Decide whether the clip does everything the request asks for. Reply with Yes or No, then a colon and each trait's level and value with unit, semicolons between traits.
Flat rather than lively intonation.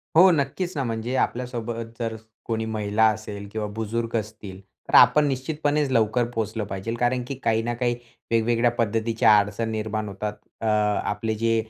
Yes: narrow, 2.0 semitones